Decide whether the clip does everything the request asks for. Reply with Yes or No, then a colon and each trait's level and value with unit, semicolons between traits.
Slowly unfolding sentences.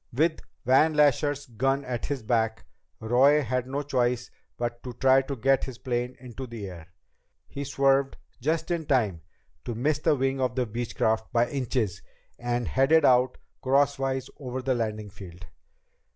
No: average, 160 wpm